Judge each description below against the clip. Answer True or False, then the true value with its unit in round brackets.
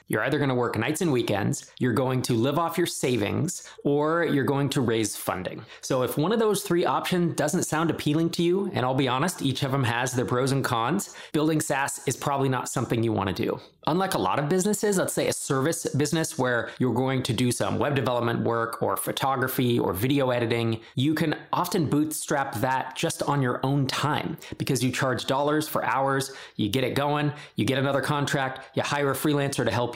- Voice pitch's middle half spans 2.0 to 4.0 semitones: True (3.7 semitones)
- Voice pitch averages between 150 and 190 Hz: False (140 Hz)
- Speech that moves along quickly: True (220 wpm)